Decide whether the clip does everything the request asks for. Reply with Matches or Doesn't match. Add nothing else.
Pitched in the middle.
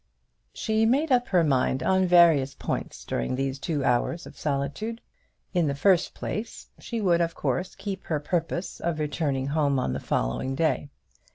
Matches